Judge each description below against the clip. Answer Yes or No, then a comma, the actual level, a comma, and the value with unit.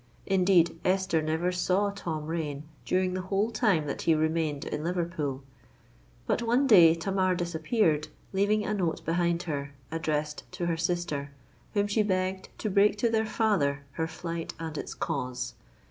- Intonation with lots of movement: No, average, 3.7 semitones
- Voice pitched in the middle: Yes, medium, 175 Hz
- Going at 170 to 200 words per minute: No, average, 160 wpm